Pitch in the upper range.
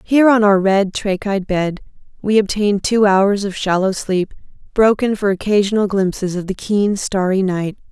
Yes: high, 200 Hz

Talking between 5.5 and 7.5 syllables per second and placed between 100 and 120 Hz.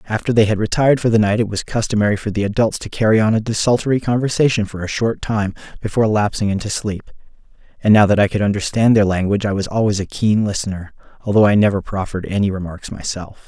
Yes: 6.6 syllables/s; low, 105 Hz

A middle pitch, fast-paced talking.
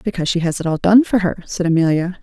Yes: medium, 180 Hz; fast, 270 wpm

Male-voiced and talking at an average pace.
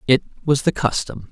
Yes: male; average, 185 wpm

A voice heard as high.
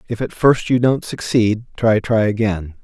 No: low, 110 Hz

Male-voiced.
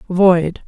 No: female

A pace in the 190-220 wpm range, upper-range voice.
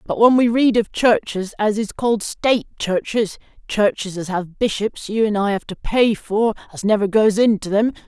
Yes: average, 195 wpm; high, 210 Hz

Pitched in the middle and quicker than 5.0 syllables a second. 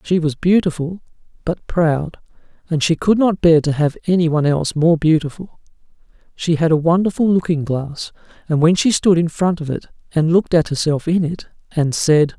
Yes: medium, 165 Hz; 5.3 syllables/s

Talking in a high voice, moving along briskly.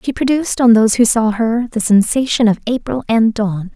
Yes: high, 230 Hz; fast, 210 wpm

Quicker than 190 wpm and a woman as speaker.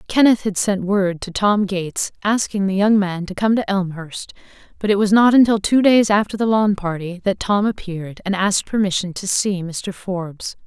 Yes: fast, 205 wpm; female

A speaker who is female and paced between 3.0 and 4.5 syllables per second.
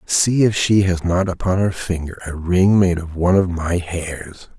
No: male; 4.4 syllables/s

